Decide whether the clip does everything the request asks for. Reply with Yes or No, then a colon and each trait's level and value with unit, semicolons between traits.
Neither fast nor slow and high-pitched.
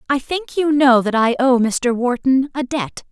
No: fast, 210 wpm; very high, 260 Hz